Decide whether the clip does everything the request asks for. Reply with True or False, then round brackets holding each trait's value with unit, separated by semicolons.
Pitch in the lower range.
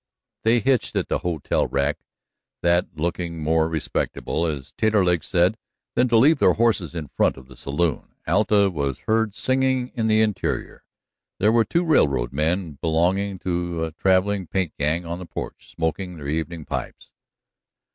True (85 Hz)